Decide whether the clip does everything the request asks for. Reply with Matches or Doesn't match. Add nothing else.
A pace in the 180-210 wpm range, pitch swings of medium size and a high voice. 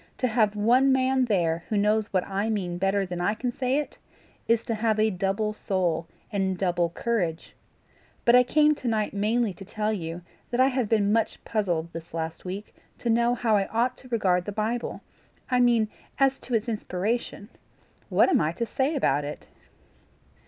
Matches